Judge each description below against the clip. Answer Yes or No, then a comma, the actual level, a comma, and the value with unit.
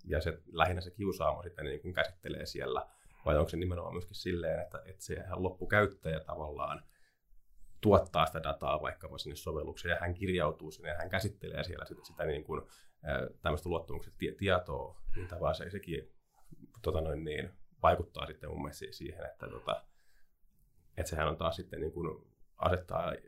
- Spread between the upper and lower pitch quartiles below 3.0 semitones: Yes, narrow, 2.6 semitones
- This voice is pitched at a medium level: No, very low, 85 Hz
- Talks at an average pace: No, fast, 170 wpm